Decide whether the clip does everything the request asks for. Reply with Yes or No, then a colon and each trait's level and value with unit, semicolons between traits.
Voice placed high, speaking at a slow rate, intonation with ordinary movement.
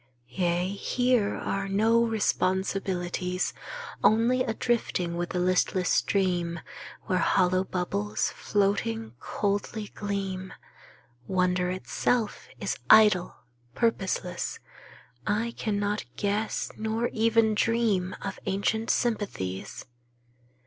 Yes: high, 195 Hz; slow, 95 wpm; average, 3.3 semitones